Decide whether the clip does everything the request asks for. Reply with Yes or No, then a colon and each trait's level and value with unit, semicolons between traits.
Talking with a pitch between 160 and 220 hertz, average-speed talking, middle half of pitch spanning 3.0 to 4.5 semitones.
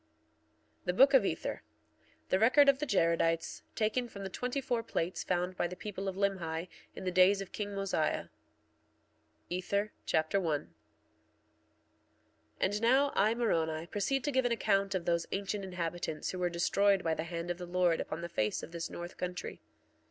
Yes: medium, 185 Hz; average, 180 wpm; average, 3.5 semitones